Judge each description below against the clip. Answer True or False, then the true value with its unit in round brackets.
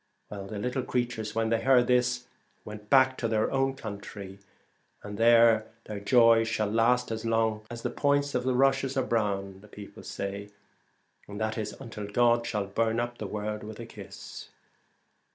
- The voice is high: False (115 Hz)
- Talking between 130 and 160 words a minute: False (175 wpm)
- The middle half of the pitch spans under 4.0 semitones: True (2.8 semitones)